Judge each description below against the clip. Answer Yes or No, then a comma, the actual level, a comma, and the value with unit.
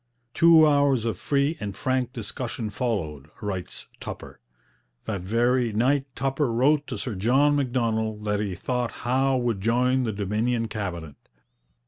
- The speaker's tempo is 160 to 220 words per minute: No, average, 140 wpm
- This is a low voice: Yes, low, 120 Hz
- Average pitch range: Yes, average, 4.0 semitones